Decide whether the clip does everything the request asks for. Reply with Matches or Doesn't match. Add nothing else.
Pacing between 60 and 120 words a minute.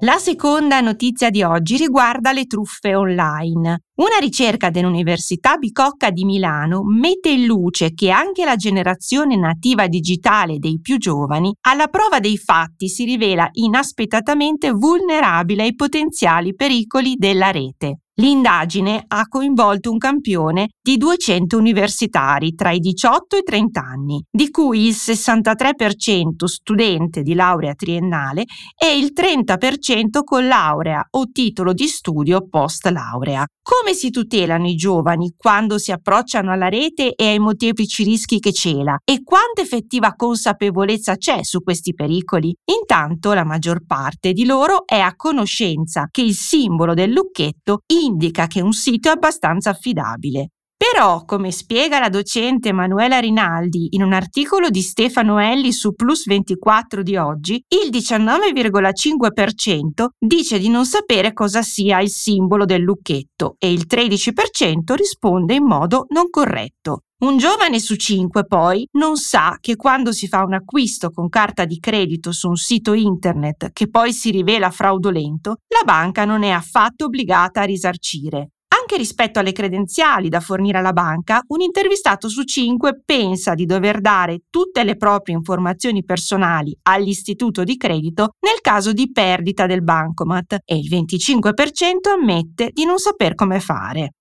Doesn't match